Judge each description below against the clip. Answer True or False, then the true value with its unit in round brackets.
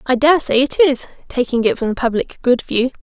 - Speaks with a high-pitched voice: True (260 Hz)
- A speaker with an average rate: False (220 wpm)